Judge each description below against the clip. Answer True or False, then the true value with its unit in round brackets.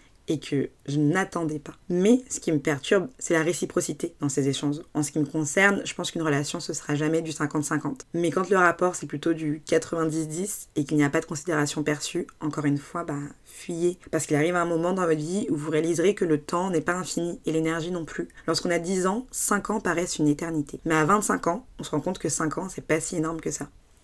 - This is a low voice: False (160 Hz)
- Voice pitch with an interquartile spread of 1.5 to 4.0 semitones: True (2.5 semitones)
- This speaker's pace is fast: True (250 wpm)